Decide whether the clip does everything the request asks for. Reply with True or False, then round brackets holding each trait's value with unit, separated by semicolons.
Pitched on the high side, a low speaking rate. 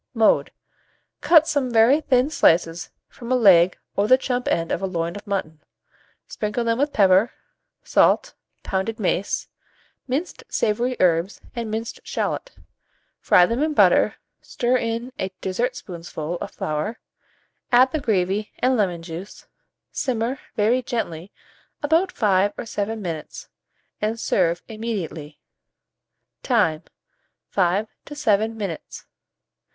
True (215 Hz; 125 wpm)